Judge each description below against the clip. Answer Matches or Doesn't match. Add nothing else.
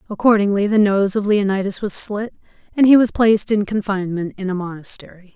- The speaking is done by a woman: Matches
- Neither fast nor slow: Matches